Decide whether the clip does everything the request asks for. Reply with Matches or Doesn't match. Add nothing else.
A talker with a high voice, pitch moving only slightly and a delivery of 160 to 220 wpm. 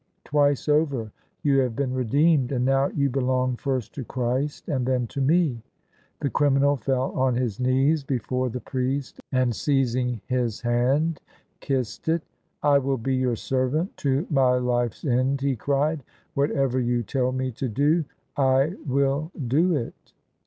Doesn't match